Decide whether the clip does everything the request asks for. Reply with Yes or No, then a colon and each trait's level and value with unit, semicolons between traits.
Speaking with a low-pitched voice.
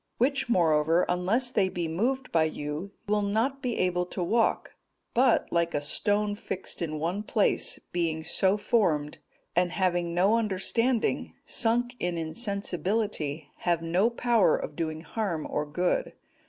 No: medium, 185 Hz